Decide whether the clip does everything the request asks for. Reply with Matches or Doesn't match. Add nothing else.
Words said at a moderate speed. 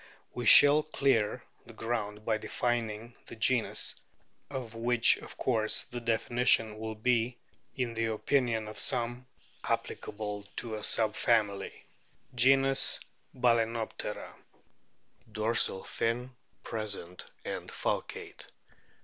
Doesn't match